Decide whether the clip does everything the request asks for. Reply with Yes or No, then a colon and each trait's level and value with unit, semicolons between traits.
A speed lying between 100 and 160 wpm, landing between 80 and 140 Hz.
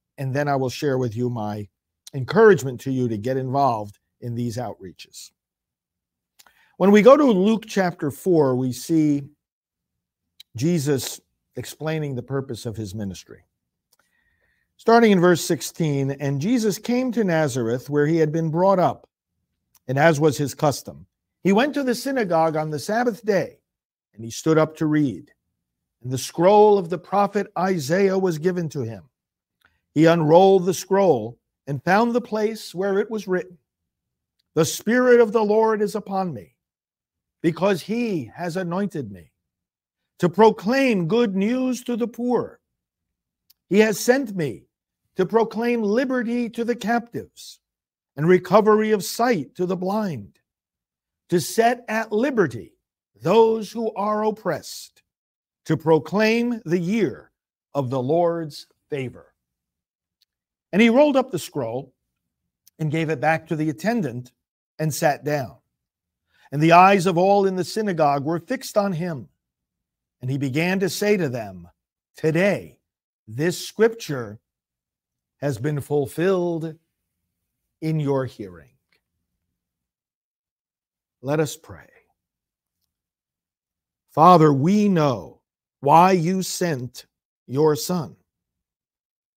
No: slow, 135 wpm; medium, 160 Hz